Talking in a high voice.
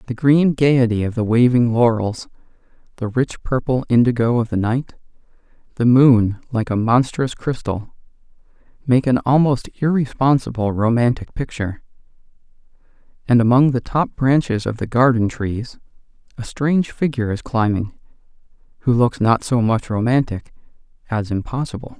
No: low, 120 Hz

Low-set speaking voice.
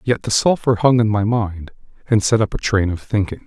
Yes: low, 110 Hz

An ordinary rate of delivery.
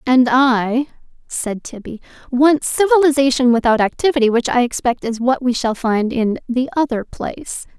Yes: average, 155 wpm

